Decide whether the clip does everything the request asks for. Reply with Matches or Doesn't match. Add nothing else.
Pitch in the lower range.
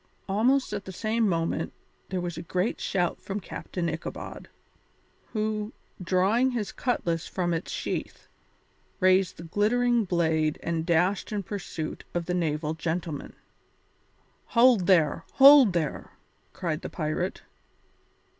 Doesn't match